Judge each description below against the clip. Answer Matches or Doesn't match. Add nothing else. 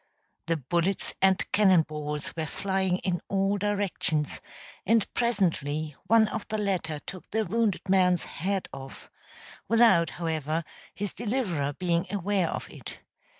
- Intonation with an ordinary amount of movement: Matches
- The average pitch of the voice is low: Doesn't match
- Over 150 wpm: Doesn't match